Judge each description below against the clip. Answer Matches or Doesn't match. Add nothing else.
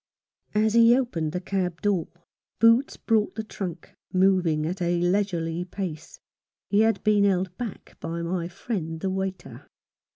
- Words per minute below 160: Matches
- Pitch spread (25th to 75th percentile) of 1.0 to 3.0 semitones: Doesn't match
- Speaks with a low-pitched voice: Doesn't match